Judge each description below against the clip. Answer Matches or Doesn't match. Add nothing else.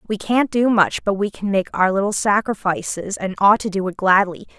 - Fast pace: Matches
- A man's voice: Doesn't match